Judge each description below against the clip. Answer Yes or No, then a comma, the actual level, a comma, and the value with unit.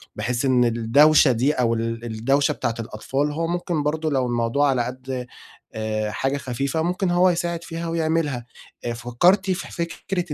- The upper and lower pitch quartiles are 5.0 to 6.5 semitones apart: Yes, wide, 5.6 semitones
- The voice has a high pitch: No, low, 135 Hz